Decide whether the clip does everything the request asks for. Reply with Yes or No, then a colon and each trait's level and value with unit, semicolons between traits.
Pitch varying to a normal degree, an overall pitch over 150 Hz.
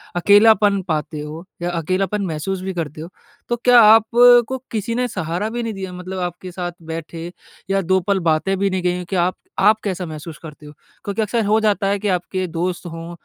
Yes: average, 3.5 semitones; medium, 185 Hz